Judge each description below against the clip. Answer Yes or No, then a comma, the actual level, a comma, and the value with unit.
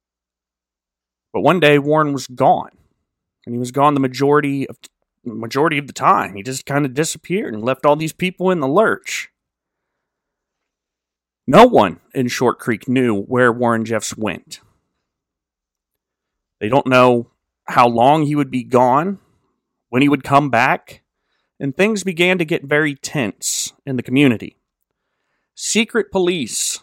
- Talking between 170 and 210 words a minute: No, average, 150 wpm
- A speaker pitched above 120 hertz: Yes, low, 135 Hz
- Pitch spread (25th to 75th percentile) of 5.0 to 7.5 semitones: No, average, 3.8 semitones